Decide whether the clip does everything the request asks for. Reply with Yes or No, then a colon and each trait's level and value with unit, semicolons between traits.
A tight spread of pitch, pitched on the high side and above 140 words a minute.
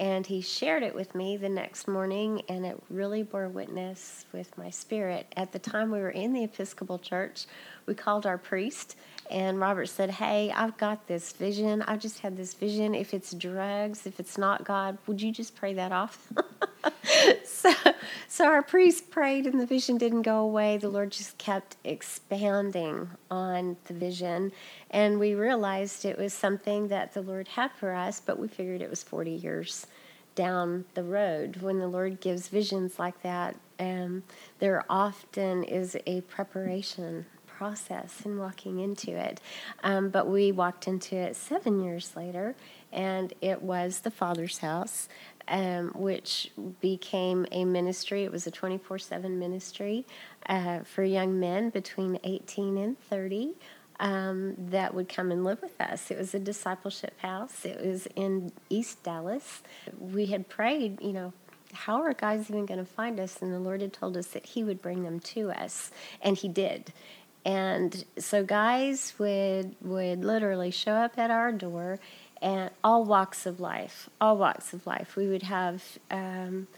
Yes: narrow, 2.1 semitones; high, 195 Hz; average, 170 wpm